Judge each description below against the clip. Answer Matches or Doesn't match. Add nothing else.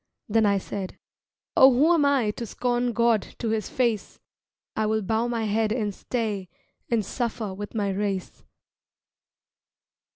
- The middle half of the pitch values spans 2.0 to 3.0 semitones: Matches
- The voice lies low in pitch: Doesn't match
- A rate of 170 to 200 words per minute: Doesn't match